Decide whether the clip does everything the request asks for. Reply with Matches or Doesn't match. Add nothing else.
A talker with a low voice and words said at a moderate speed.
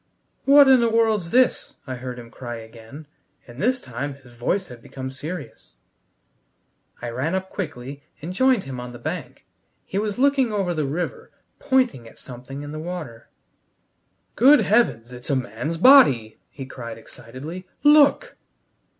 Doesn't match